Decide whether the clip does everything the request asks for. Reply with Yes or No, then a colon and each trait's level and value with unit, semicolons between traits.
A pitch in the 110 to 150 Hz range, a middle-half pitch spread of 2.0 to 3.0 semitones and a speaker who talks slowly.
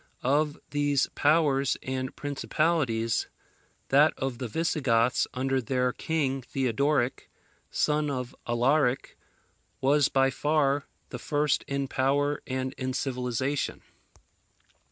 Yes: low, 135 Hz; narrow, 2.4 semitones; slow, 105 wpm